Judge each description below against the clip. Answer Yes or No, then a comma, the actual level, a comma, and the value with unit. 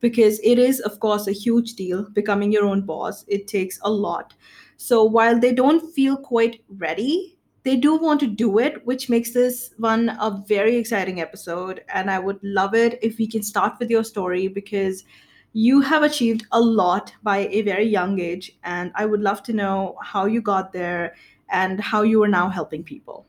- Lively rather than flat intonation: No, average, 3.1 semitones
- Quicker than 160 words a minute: Yes, average, 200 wpm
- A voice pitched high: Yes, high, 210 Hz